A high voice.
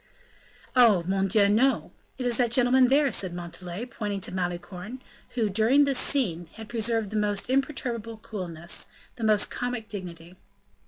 Yes: high, 215 Hz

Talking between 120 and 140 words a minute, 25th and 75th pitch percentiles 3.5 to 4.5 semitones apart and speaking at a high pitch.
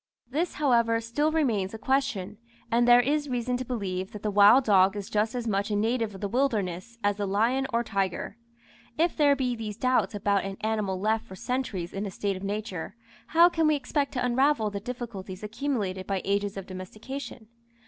No: average, 200 wpm; average, 4.2 semitones; high, 220 Hz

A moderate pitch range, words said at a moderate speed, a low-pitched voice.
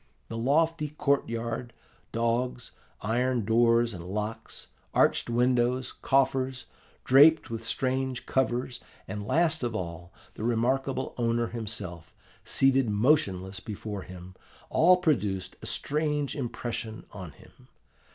No: average, 3.6 semitones; slow, 115 wpm; low, 120 Hz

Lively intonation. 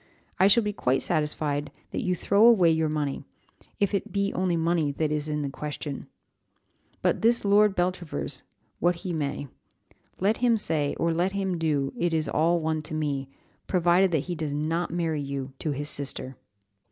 No: average, 3.8 semitones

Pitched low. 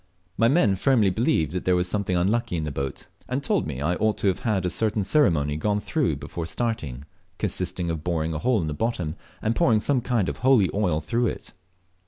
Yes: low, 100 Hz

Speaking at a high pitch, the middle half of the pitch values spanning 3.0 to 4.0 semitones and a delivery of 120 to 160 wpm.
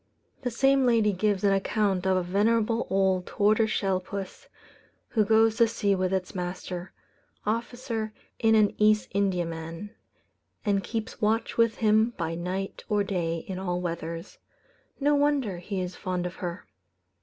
Yes: high, 200 Hz; average, 3.4 semitones; average, 155 wpm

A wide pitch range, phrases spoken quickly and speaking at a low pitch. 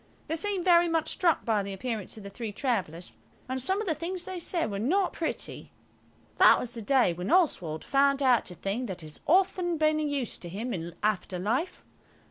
No: wide, 9.0 semitones; fast, 210 wpm; very high, 255 Hz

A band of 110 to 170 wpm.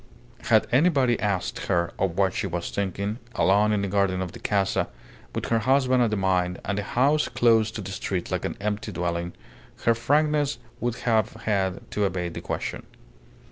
No: average, 185 wpm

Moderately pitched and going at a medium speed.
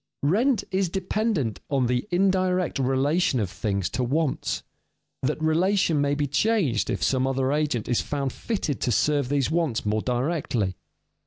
Yes: medium, 145 Hz; average, 160 wpm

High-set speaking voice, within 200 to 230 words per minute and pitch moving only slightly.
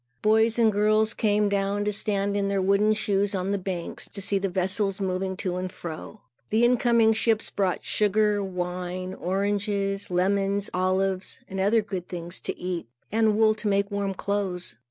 No: high, 200 Hz; average, 175 wpm; narrow, 2.0 semitones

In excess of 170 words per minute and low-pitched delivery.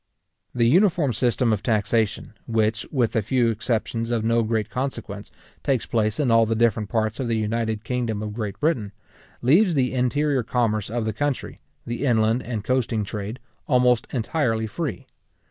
No: average, 165 wpm; low, 115 Hz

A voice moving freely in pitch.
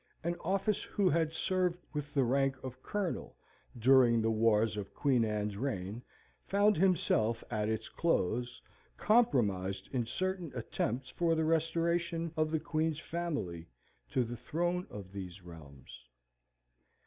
Yes: wide, 7.6 semitones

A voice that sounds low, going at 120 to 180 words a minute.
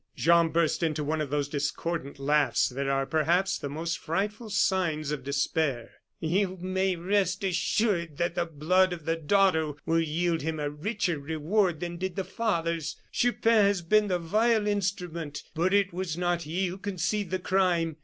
No: medium, 170 Hz; average, 175 wpm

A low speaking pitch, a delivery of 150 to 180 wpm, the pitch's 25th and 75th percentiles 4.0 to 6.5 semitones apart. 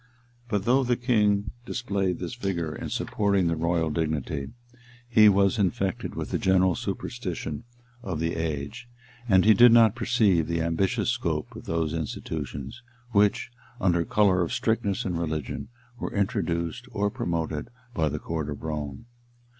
Yes: very low, 95 Hz; average, 155 wpm; average, 4.9 semitones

